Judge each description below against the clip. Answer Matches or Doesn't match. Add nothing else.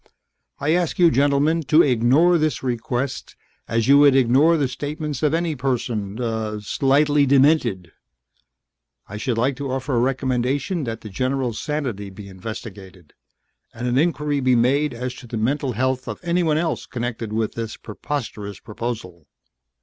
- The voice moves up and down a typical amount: Matches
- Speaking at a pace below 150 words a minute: Doesn't match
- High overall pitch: Doesn't match